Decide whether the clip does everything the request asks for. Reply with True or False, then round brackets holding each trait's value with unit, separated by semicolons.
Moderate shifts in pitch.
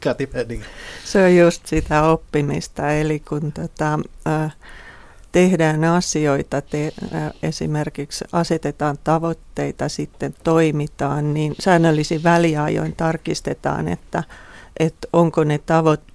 False (1.8 semitones)